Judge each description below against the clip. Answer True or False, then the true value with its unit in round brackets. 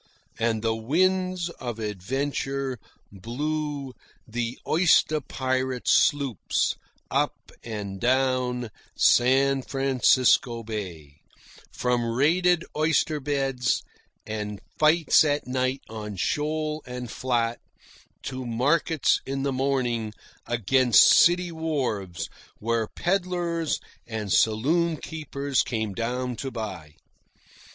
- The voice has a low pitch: True (130 Hz)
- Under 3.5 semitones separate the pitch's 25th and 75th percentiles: False (4.5 semitones)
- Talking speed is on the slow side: True (95 wpm)